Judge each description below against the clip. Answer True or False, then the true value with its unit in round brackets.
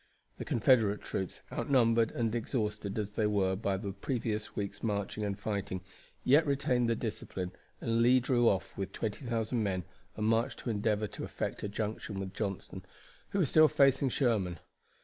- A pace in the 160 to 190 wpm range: True (170 wpm)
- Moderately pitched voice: False (110 Hz)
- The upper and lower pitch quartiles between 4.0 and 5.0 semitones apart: False (3.0 semitones)